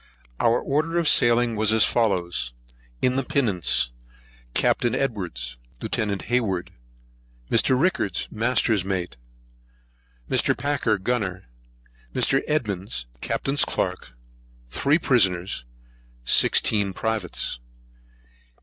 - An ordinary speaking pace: No, slow, 95 wpm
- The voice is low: Yes, low, 110 Hz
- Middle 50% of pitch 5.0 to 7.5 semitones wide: Yes, wide, 5.5 semitones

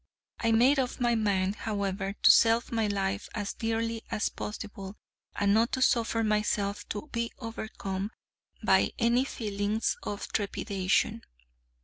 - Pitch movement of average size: No, narrow, 2.3 semitones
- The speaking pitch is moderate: No, high, 215 Hz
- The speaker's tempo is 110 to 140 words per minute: Yes, slow, 135 wpm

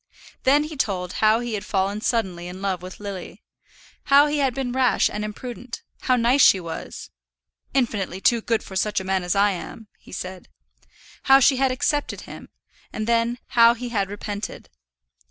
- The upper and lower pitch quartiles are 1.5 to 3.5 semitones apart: No, average, 4.5 semitones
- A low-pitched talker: No, high, 220 Hz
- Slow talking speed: No, average, 180 wpm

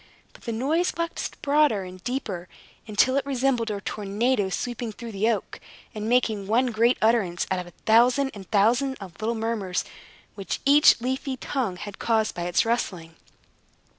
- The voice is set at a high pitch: Yes, high, 225 Hz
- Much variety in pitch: No, average, 4.3 semitones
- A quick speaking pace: No, average, 165 wpm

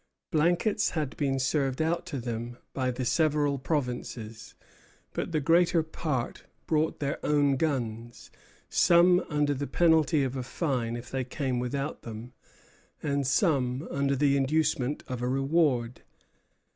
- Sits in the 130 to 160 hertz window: Yes, medium, 140 Hz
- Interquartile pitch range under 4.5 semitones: Yes, average, 3.7 semitones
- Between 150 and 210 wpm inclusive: No, average, 140 wpm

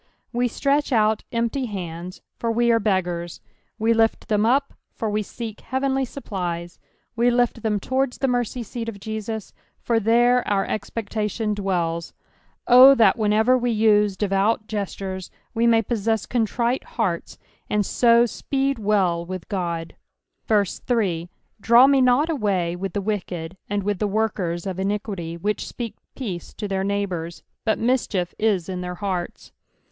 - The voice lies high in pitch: Yes, high, 210 Hz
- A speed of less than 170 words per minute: Yes, average, 150 wpm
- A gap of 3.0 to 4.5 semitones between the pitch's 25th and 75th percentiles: Yes, average, 3.7 semitones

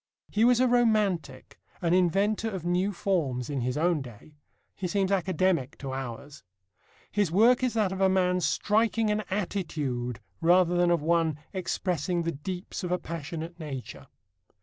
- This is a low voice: No, medium, 180 Hz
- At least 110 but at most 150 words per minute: No, average, 160 wpm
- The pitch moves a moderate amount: Yes, average, 4.4 semitones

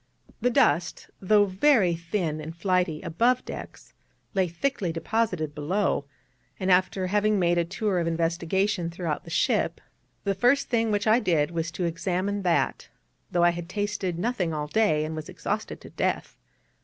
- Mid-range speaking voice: Yes, medium, 180 Hz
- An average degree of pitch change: Yes, average, 3.7 semitones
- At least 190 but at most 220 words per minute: No, average, 165 wpm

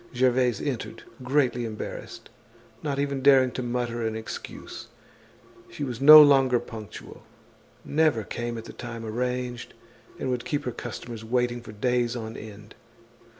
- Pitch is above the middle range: No, low, 120 Hz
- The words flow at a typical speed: Yes, average, 145 wpm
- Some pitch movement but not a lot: No, narrow, 2.3 semitones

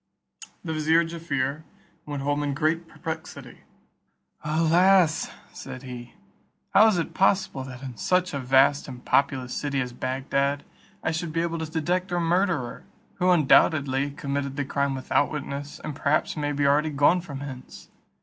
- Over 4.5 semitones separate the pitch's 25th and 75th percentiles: No, average, 3.3 semitones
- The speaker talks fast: No, average, 160 wpm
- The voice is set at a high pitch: No, medium, 145 Hz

